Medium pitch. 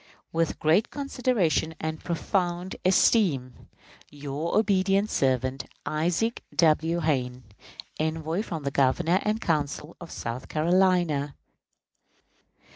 Yes: medium, 160 Hz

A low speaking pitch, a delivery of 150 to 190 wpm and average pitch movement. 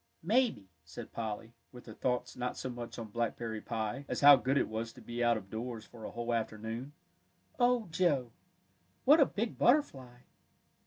Yes: low, 120 Hz; average, 175 wpm; average, 4.0 semitones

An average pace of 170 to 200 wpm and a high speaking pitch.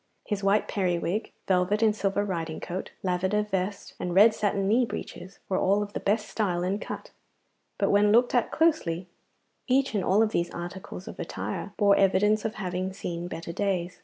Yes: average, 185 wpm; high, 195 Hz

